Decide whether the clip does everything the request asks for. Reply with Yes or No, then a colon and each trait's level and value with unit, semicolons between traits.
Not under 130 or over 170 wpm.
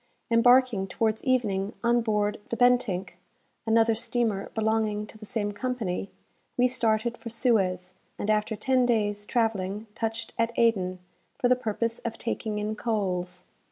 Yes: average, 145 wpm